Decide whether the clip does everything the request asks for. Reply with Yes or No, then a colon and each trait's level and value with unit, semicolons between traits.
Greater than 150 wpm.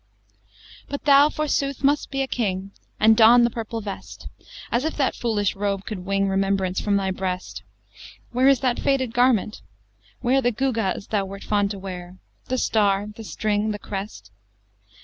Yes: average, 170 wpm